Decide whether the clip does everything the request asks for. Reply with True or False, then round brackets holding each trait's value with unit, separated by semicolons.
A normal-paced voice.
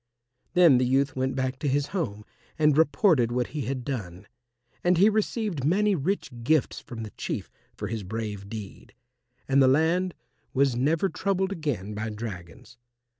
True (165 wpm)